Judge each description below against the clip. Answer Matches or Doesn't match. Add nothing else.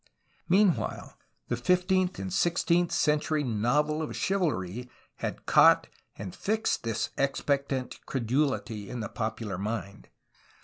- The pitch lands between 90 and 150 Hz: Matches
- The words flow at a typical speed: Doesn't match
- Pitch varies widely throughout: Matches